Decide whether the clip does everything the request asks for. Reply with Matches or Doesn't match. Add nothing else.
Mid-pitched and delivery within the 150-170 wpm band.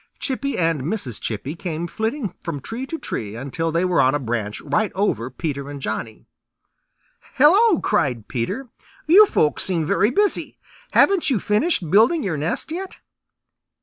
Matches